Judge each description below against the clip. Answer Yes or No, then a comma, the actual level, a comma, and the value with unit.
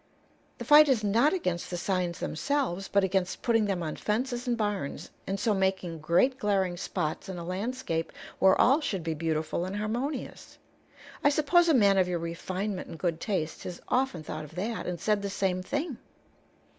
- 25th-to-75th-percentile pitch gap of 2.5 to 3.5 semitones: No, average, 5.3 semitones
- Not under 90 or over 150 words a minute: No, average, 185 wpm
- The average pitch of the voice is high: Yes, high, 195 Hz